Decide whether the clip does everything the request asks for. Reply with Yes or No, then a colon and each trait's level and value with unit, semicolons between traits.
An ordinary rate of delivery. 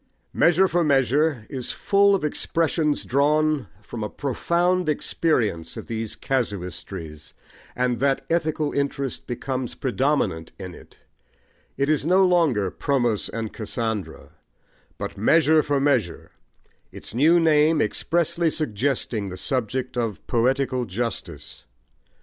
No: slow, 120 wpm